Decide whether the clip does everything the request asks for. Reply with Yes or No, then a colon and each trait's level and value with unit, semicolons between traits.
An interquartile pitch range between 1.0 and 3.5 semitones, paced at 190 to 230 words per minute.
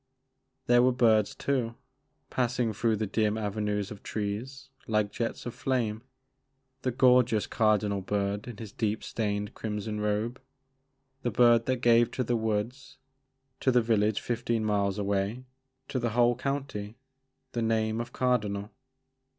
No: average, 2.9 semitones; average, 150 wpm